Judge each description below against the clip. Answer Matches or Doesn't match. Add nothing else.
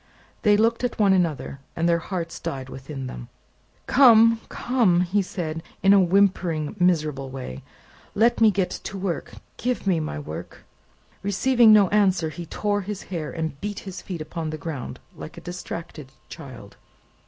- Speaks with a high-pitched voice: Doesn't match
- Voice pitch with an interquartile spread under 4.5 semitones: Doesn't match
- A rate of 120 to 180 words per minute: Matches